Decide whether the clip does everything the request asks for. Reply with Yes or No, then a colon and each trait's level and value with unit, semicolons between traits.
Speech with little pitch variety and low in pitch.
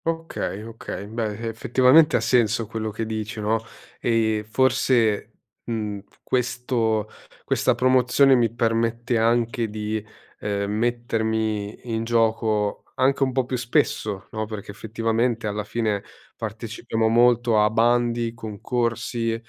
Yes: narrow, 1.8 semitones; low, 115 Hz